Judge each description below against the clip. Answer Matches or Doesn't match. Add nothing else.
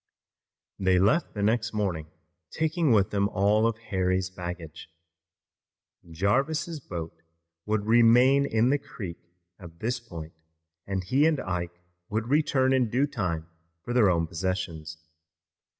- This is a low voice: Matches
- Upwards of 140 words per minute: Doesn't match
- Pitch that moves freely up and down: Matches